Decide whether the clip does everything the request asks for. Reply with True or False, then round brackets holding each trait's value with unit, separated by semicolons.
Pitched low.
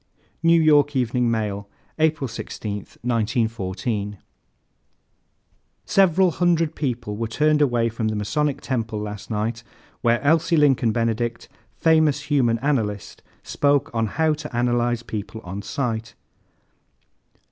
True (120 Hz)